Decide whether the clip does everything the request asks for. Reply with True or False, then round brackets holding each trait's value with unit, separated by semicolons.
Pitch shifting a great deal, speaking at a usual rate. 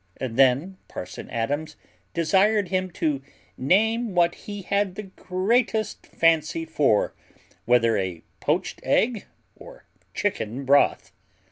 False (6.8 semitones; 110 wpm)